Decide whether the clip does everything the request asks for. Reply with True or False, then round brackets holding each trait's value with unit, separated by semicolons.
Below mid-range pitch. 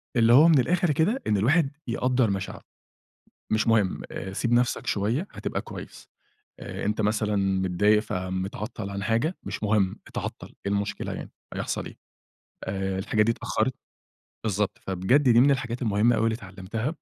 True (110 Hz)